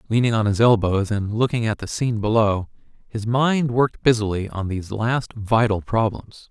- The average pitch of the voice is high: No, low, 110 Hz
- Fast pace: No, average, 175 wpm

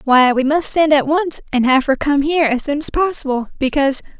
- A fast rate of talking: Yes, fast, 230 wpm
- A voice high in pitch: Yes, very high, 285 Hz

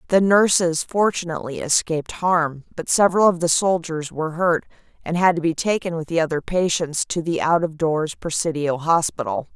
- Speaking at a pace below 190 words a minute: Yes, average, 175 wpm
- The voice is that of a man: No, female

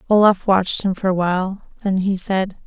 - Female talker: Yes, female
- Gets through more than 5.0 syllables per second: Yes, 5.5 syllables/s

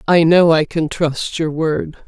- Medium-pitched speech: Yes, medium, 160 Hz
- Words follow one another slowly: No, average, 200 wpm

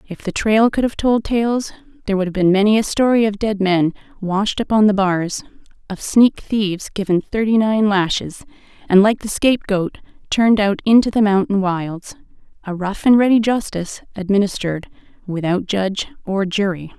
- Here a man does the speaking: No, female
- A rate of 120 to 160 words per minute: No, average, 170 wpm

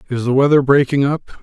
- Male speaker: Yes, male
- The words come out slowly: No, fast, 210 wpm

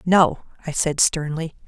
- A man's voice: No, female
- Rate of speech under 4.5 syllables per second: Yes, 3.9 syllables/s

